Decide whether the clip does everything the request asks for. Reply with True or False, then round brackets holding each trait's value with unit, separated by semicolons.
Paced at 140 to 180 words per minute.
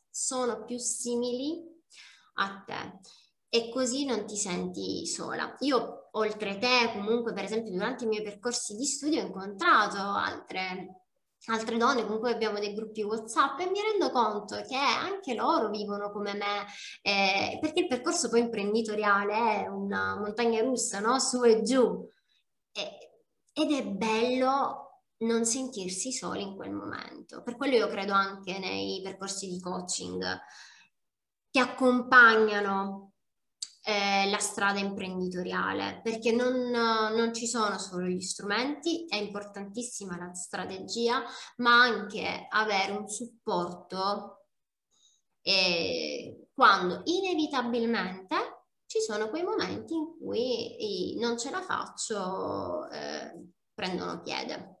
False (125 wpm)